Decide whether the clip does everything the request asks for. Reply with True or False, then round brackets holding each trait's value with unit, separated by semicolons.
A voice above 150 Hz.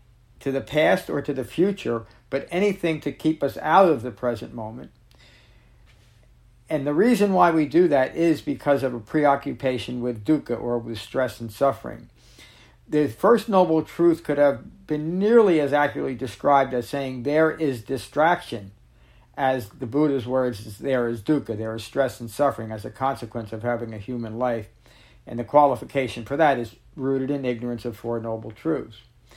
False (130 Hz)